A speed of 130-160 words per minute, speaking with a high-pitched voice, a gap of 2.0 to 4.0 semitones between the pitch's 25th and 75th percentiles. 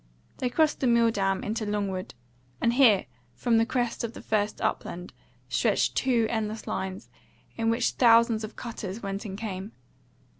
Yes: average, 155 wpm; high, 225 Hz; average, 2.7 semitones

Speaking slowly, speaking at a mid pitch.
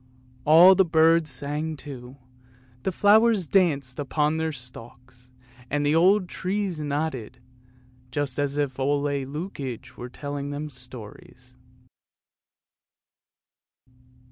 Yes: slow, 110 wpm; medium, 145 Hz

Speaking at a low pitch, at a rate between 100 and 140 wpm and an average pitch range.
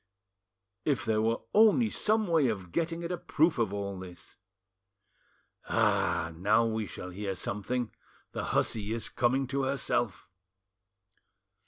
No: low, 115 Hz; slow, 135 wpm; wide, 7.0 semitones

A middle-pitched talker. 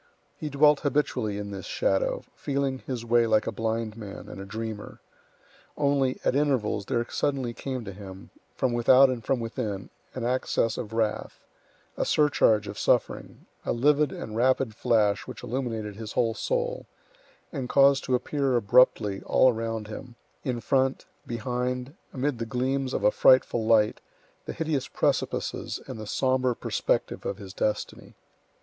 No: low, 120 Hz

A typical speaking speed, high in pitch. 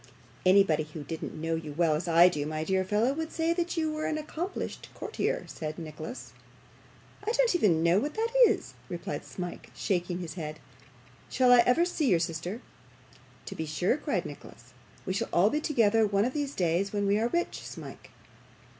Yes: average, 190 wpm; high, 195 Hz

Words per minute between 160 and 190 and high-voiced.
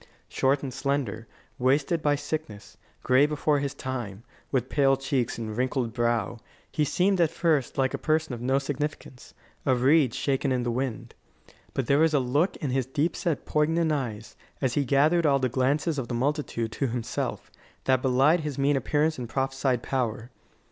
No: average, 180 wpm; low, 135 Hz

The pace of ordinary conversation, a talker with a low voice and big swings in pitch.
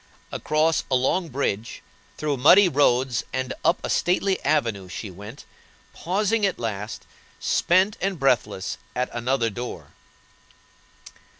No: slow, 120 wpm; low, 130 Hz; wide, 7.2 semitones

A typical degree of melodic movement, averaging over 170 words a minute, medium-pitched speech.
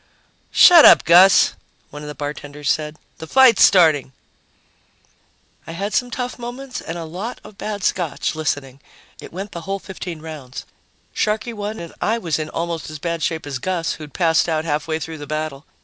Yes: average, 4.4 semitones; average, 180 wpm; medium, 165 Hz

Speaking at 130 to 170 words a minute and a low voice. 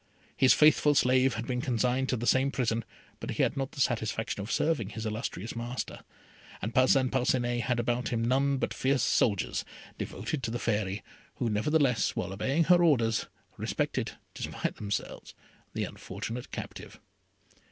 Yes: average, 160 wpm; low, 125 Hz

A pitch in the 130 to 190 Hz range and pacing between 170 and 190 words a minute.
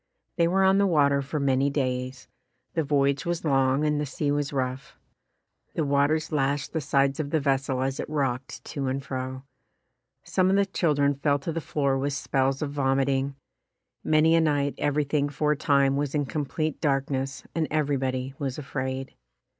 Yes: medium, 140 Hz; average, 180 wpm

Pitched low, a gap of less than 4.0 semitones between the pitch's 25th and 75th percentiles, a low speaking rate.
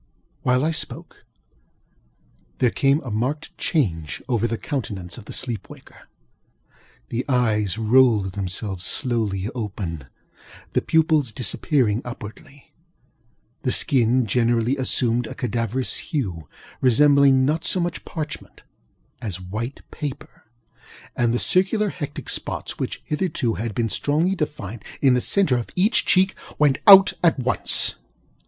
No: low, 125 Hz; average, 5.1 semitones; slow, 130 wpm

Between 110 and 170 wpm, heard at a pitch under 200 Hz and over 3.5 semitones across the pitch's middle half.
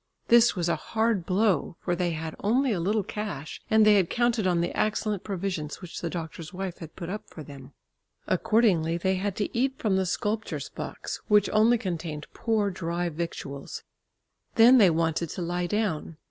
No: average, 185 wpm; medium, 185 Hz; average, 4.2 semitones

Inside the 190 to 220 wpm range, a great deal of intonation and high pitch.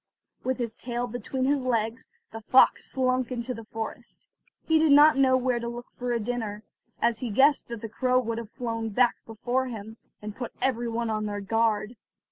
No: average, 200 wpm; narrow, 2.3 semitones; high, 235 Hz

